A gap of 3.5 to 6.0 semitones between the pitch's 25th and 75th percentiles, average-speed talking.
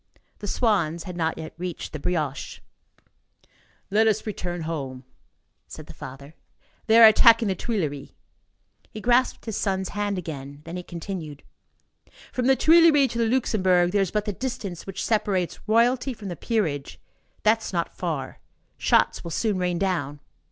Yes: average, 5.2 semitones; average, 160 wpm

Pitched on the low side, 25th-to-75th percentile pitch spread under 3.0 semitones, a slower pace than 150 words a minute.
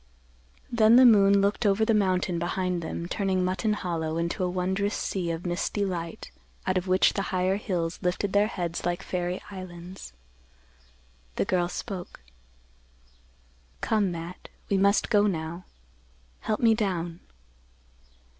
No: medium, 185 Hz; narrow, 2.5 semitones; average, 140 wpm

